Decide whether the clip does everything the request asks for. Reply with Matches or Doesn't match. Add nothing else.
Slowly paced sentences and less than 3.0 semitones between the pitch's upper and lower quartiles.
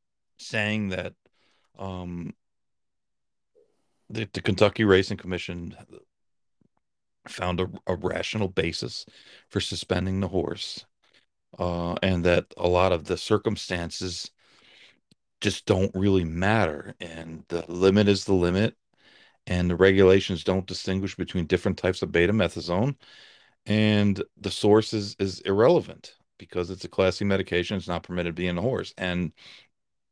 Matches